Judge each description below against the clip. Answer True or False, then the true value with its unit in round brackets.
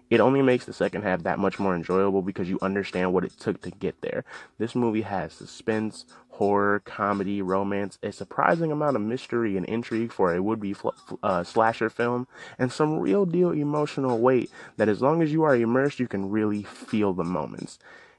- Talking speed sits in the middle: True (195 wpm)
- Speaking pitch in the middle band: False (110 Hz)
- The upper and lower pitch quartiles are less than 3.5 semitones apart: False (4.1 semitones)